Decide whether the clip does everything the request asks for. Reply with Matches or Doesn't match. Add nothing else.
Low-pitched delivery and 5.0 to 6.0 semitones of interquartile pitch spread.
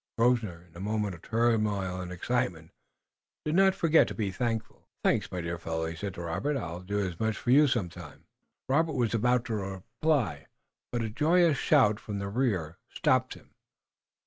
Matches